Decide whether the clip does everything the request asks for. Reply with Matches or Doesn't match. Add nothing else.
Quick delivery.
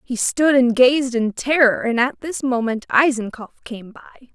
Doesn't match